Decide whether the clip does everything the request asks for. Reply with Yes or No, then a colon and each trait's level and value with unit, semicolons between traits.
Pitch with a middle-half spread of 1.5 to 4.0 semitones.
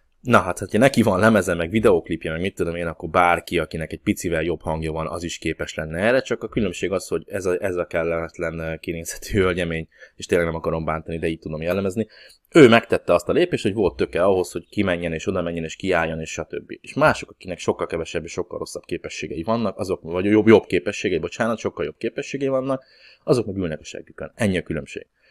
No: average, 4.4 semitones